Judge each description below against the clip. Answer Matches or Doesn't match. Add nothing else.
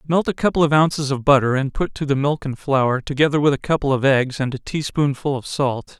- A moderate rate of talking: Doesn't match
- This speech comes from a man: Matches